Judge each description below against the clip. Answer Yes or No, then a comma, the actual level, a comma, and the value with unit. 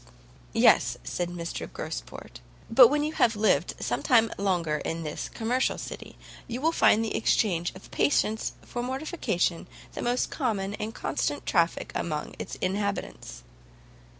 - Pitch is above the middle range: Yes, high, 210 Hz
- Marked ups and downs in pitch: Yes, wide, 6.1 semitones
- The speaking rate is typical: Yes, average, 145 wpm